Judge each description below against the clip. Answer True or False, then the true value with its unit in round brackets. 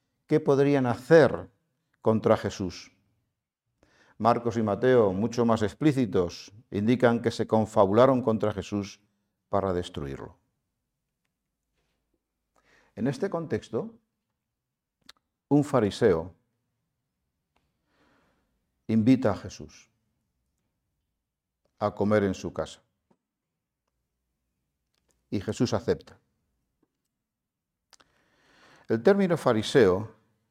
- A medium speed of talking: False (75 wpm)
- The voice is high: False (110 Hz)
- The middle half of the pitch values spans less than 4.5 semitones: True (4.1 semitones)